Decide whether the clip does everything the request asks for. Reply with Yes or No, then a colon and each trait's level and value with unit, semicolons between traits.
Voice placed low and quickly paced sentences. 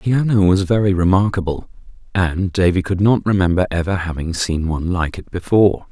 No: very low, 90 Hz; average, 175 wpm